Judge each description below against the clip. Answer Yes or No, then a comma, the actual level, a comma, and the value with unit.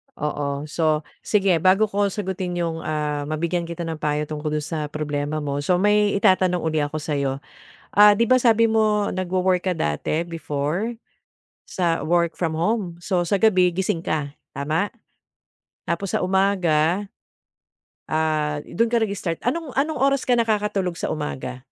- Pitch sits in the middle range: Yes, medium, 175 Hz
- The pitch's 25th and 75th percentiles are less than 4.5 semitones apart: No, average, 4.8 semitones